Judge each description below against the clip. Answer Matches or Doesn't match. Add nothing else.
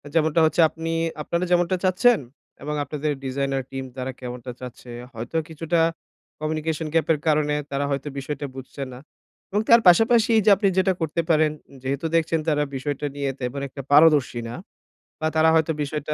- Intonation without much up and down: Doesn't match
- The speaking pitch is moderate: Matches